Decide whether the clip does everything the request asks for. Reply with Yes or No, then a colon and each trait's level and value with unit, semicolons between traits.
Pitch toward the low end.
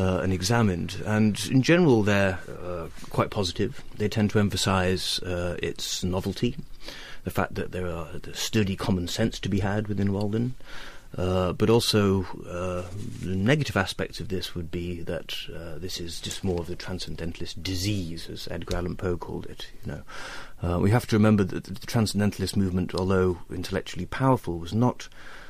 Yes: very low, 95 Hz